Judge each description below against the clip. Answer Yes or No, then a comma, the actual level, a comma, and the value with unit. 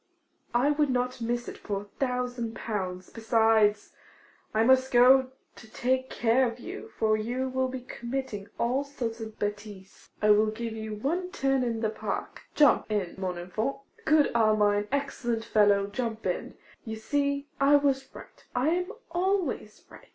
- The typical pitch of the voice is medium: No, high, 235 Hz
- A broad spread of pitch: No, average, 3.7 semitones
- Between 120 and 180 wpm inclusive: Yes, average, 165 wpm